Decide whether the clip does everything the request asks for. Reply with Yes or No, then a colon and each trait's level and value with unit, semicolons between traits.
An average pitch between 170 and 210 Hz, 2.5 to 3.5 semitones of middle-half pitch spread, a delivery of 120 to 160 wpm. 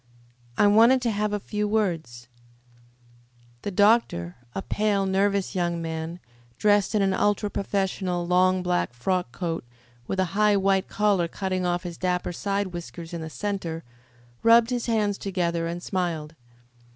Yes: high, 190 Hz; average, 3.0 semitones; average, 150 wpm